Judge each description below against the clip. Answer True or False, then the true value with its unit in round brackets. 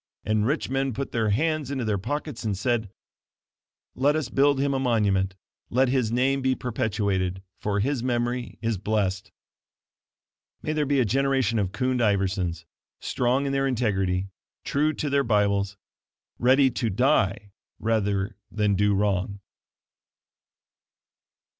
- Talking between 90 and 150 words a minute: True (140 wpm)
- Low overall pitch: True (115 Hz)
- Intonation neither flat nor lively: True (4.9 semitones)